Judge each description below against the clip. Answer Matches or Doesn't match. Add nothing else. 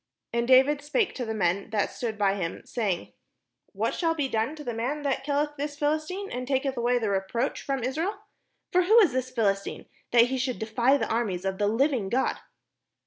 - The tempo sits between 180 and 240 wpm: Matches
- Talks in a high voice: Matches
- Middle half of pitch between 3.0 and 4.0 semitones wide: Doesn't match